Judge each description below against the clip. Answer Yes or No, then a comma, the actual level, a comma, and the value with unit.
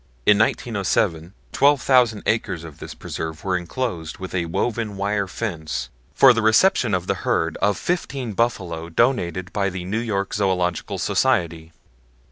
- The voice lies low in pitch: Yes, low, 100 Hz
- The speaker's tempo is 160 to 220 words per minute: No, average, 145 wpm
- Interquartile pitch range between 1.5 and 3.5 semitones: No, average, 4.9 semitones